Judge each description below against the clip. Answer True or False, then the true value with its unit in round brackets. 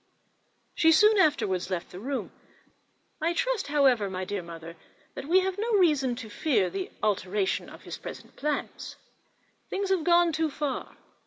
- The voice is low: False (290 Hz)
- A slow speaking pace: False (160 wpm)